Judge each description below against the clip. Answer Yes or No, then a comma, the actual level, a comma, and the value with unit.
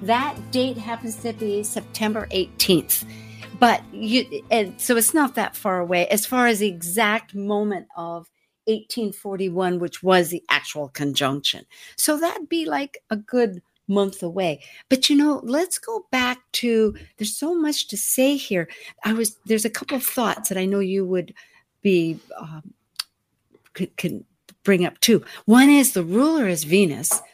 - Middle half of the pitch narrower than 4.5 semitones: No, average, 4.9 semitones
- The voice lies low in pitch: No, high, 215 Hz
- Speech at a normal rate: Yes, average, 160 wpm